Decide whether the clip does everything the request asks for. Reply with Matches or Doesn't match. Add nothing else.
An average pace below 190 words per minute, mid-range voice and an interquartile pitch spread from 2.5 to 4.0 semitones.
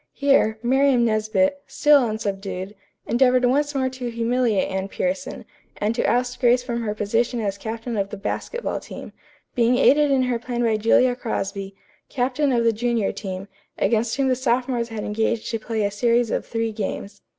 Doesn't match